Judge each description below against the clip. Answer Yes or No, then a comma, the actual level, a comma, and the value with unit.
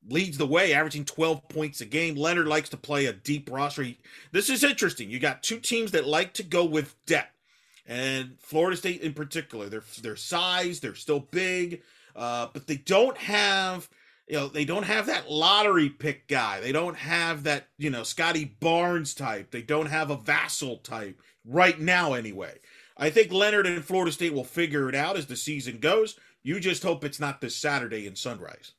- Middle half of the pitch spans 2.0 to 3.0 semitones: No, average, 3.7 semitones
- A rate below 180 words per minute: No, average, 200 wpm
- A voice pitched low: No, medium, 155 Hz